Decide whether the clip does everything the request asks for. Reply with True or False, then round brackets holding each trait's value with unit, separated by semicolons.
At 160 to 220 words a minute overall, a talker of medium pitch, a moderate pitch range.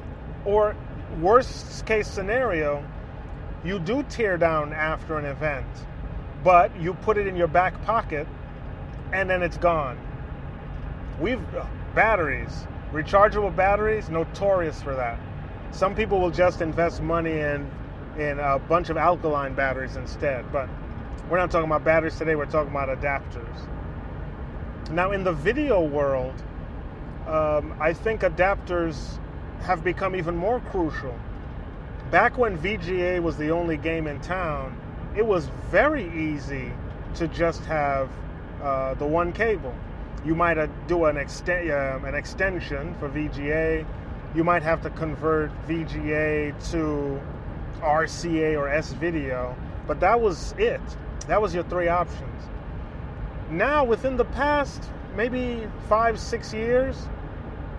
False (135 wpm; 160 Hz; 4.5 semitones)